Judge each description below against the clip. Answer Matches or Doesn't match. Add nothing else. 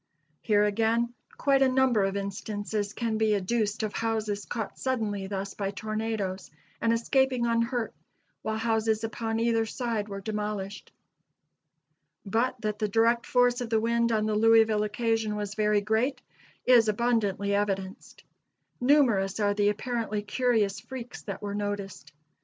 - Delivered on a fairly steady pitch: Matches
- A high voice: Matches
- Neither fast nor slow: Matches